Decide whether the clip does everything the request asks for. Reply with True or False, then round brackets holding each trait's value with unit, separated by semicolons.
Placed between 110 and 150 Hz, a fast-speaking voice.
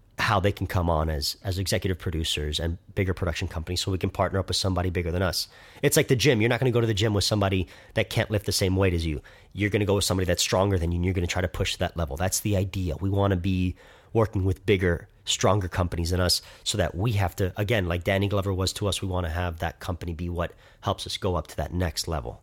False (95 Hz; 275 wpm)